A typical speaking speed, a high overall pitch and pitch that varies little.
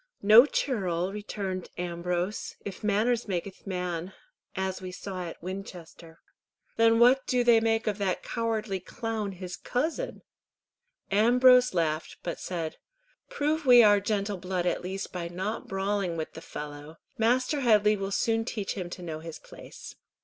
No: average, 150 wpm; high, 195 Hz; average, 4.0 semitones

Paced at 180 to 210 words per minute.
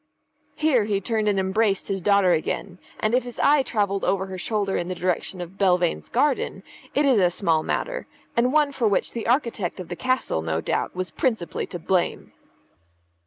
Yes: average, 190 wpm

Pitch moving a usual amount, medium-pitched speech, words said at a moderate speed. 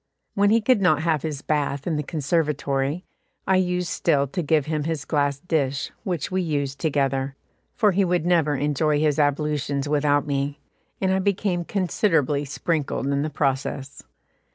Yes: average, 3.7 semitones; medium, 150 Hz; average, 165 wpm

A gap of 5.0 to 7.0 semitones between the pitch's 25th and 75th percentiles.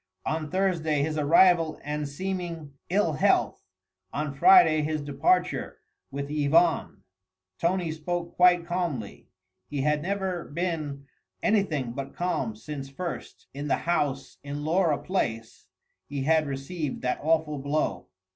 No: average, 3.6 semitones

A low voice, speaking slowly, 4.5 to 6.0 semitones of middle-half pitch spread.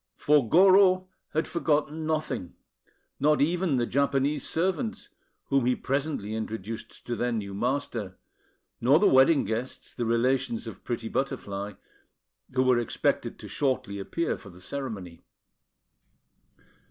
Yes: low, 130 Hz; slow, 130 wpm; average, 5.1 semitones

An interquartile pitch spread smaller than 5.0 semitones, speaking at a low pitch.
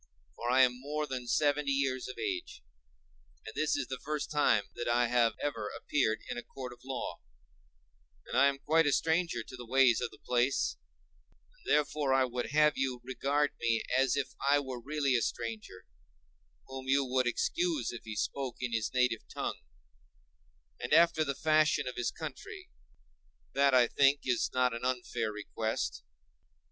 Yes: average, 3.0 semitones; low, 130 Hz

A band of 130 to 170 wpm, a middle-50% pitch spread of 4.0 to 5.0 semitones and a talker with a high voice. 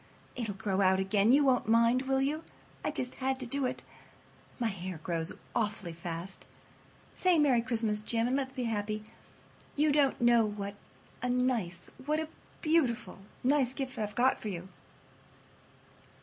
Yes: average, 150 wpm; average, 4.5 semitones; high, 235 Hz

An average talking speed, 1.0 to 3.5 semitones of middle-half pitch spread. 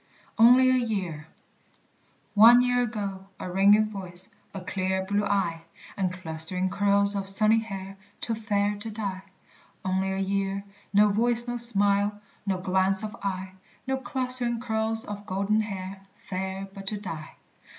Yes: average, 150 wpm; narrow, 2.6 semitones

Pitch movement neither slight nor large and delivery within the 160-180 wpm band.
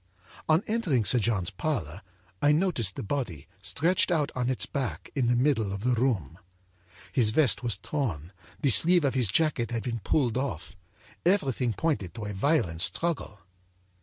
No: wide, 6.4 semitones; average, 165 wpm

